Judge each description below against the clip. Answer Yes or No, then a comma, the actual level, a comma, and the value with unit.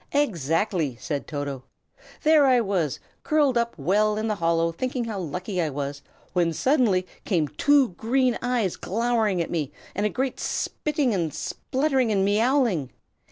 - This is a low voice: No, high, 205 Hz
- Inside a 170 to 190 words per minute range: No, average, 155 wpm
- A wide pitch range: Yes, wide, 7.1 semitones